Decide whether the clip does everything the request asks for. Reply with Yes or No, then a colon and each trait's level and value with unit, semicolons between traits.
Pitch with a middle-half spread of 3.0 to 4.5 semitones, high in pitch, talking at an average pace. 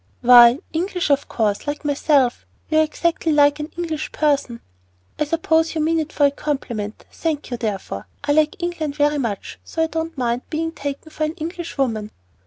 Yes: average, 3.9 semitones; very high, 295 Hz; average, 190 wpm